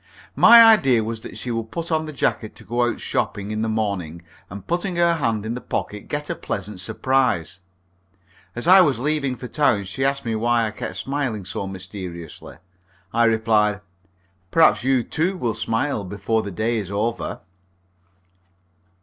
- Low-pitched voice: Yes, low, 115 Hz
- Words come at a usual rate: Yes, average, 175 wpm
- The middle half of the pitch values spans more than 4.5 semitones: Yes, average, 5.0 semitones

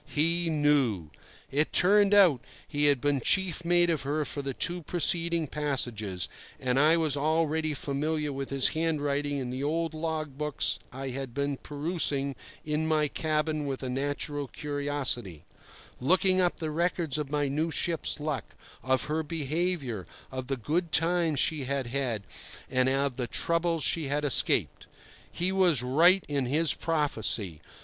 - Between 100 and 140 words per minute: No, average, 155 wpm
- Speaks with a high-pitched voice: No, medium, 150 Hz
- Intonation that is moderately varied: Yes, average, 3.1 semitones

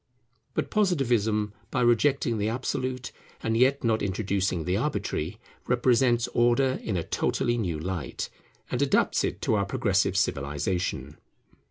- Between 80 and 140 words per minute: Yes, slow, 135 wpm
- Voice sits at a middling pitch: No, low, 110 Hz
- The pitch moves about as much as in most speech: Yes, average, 4.5 semitones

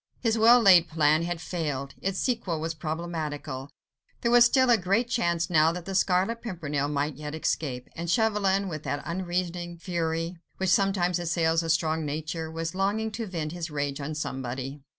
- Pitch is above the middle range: No, medium, 170 Hz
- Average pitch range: Yes, average, 3.7 semitones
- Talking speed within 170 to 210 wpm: Yes, average, 175 wpm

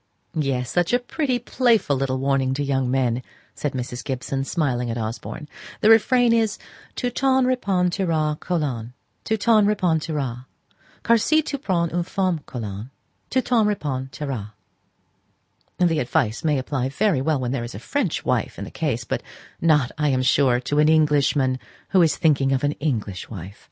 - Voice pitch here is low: No, medium, 145 Hz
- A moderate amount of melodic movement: No, wide, 6.3 semitones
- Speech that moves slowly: No, average, 170 wpm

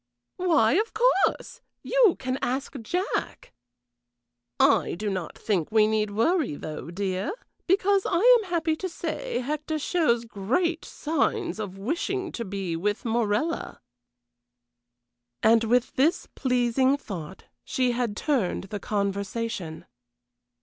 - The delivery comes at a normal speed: No, slow, 120 wpm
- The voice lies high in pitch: Yes, high, 245 Hz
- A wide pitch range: Yes, wide, 8.5 semitones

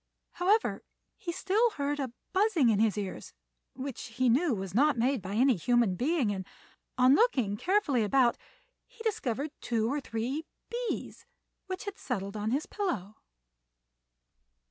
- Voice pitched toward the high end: Yes, very high, 260 Hz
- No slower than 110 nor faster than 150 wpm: Yes, average, 145 wpm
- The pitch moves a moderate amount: No, wide, 7.8 semitones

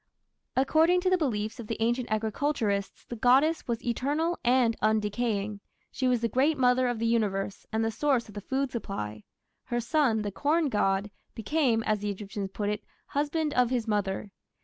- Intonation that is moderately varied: Yes, average, 4.3 semitones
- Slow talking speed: No, average, 180 wpm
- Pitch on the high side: Yes, high, 235 Hz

